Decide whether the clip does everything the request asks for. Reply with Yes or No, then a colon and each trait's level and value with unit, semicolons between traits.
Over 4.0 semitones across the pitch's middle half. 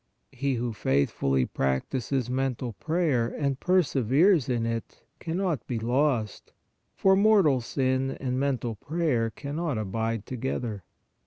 Yes: average, 4.4 semitones